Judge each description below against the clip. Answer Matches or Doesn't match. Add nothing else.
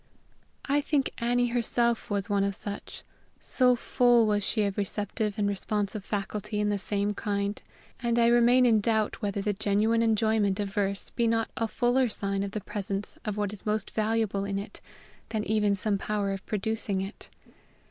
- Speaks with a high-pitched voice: Matches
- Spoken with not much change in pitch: Matches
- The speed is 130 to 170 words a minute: Doesn't match